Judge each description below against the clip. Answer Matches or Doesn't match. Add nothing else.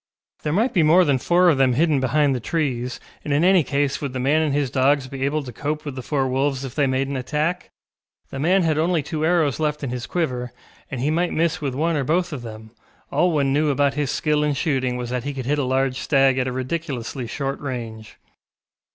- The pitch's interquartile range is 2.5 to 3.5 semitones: Matches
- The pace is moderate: Doesn't match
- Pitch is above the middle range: Doesn't match